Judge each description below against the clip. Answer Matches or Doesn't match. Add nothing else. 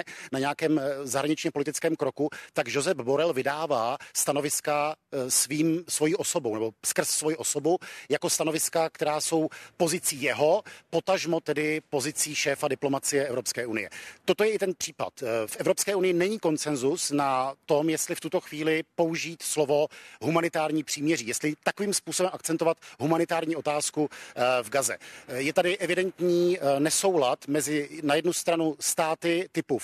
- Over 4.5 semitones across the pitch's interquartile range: Doesn't match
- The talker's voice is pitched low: Doesn't match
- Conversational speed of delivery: Matches